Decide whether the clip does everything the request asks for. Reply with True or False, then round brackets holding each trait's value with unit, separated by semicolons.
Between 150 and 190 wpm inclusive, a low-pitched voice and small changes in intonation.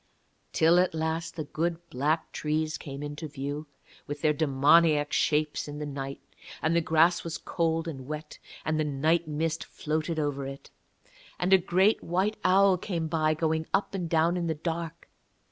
False (175 wpm; 160 Hz; 2.1 semitones)